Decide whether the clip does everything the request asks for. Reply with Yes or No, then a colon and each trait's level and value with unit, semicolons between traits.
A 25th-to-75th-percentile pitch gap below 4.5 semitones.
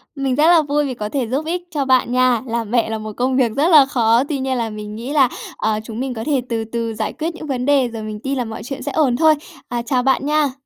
Yes: average, 3.8 semitones